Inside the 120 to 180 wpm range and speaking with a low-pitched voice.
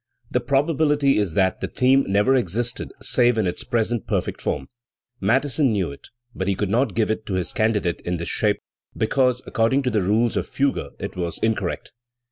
No: average, 190 wpm; low, 115 Hz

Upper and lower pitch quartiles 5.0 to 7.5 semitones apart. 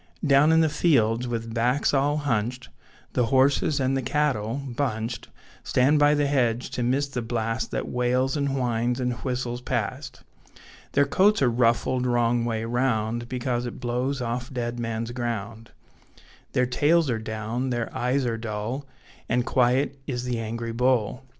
No: narrow, 2.5 semitones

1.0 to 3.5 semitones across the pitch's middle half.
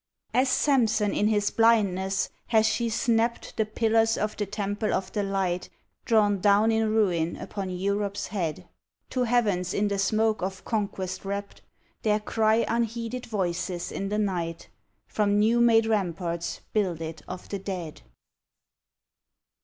Yes: average, 2.8 semitones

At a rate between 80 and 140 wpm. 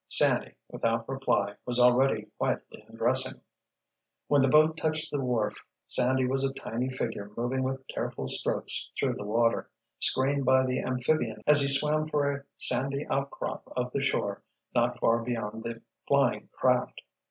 No: average, 155 wpm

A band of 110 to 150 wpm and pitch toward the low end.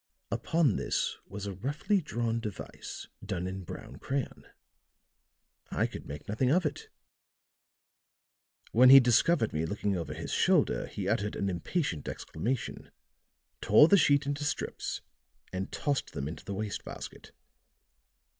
Yes: slow, 135 wpm; low, 110 Hz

